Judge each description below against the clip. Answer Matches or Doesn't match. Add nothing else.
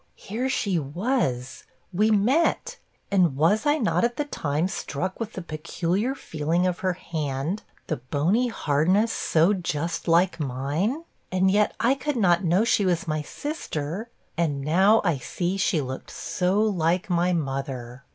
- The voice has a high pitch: Doesn't match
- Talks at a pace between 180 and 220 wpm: Doesn't match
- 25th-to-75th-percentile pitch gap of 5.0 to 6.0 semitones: Matches